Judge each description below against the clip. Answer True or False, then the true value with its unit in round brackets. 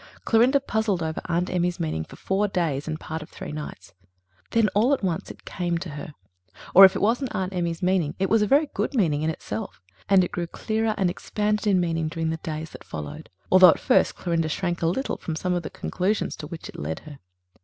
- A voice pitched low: False (175 Hz)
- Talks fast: True (230 wpm)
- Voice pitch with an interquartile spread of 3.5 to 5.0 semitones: True (4.0 semitones)